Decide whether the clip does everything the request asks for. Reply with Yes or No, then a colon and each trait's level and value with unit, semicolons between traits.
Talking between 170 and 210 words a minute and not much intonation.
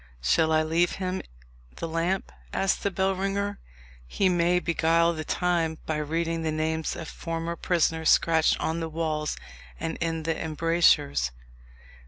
No: average, 145 wpm; narrow, 1.6 semitones